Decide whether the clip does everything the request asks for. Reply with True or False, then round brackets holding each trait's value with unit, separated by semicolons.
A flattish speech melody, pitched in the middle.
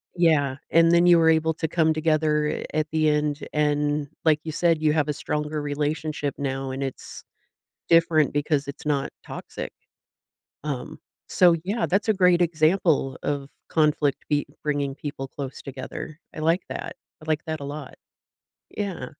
True (2.0 semitones; 150 Hz)